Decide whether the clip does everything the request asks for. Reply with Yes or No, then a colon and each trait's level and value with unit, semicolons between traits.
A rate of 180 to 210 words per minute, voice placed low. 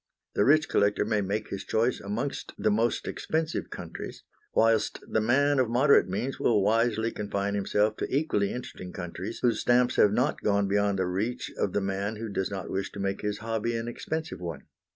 Yes: average, 195 wpm; low, 105 Hz